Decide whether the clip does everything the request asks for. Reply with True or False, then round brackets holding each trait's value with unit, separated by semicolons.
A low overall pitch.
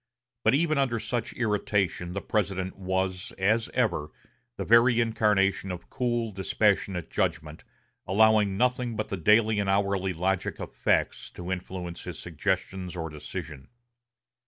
True (95 Hz)